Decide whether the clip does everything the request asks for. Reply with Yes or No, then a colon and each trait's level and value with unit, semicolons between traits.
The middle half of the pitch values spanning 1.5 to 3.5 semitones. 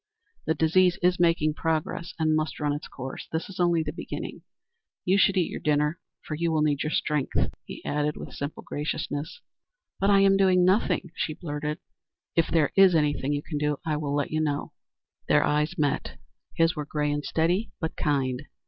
Yes: average, 2.8 semitones